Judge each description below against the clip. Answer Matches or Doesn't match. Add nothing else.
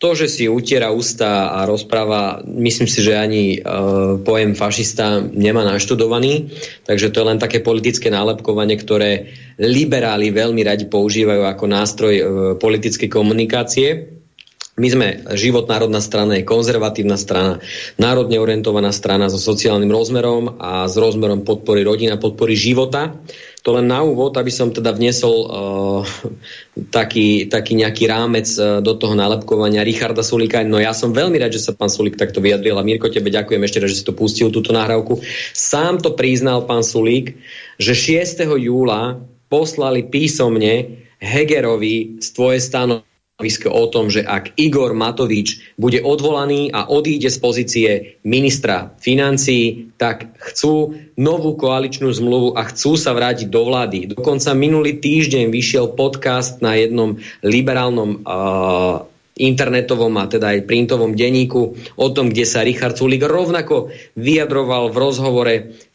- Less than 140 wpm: Doesn't match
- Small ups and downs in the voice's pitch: Doesn't match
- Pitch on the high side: Doesn't match